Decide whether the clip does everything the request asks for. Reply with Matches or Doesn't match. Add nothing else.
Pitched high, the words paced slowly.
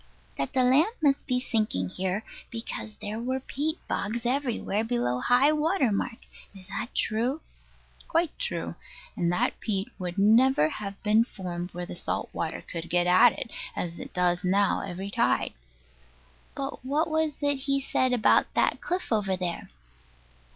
Doesn't match